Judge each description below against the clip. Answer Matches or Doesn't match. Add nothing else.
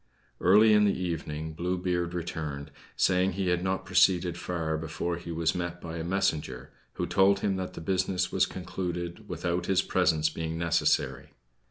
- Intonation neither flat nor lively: Doesn't match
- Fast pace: Doesn't match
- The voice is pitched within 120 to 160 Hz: Doesn't match